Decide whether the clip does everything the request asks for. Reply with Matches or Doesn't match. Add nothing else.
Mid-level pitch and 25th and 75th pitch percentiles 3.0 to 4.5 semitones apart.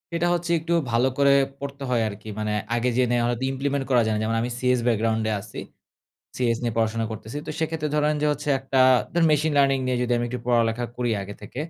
Doesn't match